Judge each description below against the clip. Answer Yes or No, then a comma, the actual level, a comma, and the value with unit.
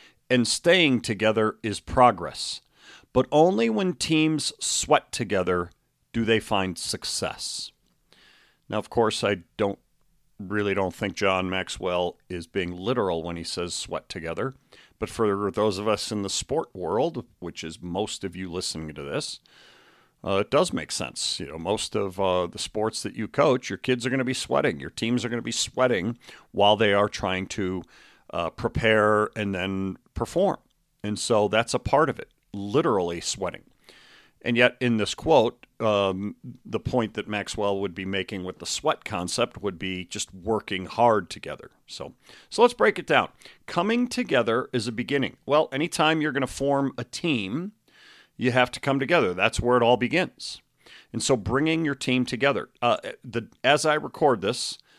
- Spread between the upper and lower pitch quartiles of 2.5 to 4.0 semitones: No, average, 4.9 semitones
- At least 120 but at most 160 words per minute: No, average, 175 wpm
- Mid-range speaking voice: No, low, 110 Hz